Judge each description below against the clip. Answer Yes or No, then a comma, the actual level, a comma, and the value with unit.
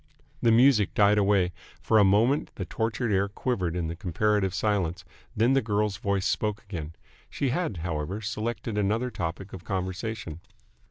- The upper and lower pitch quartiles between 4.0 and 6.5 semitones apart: No, average, 3.0 semitones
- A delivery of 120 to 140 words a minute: No, average, 155 wpm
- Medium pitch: No, low, 105 Hz